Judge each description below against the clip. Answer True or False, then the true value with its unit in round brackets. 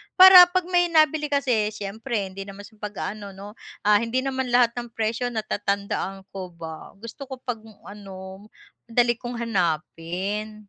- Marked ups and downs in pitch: False (3.9 semitones)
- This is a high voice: True (215 Hz)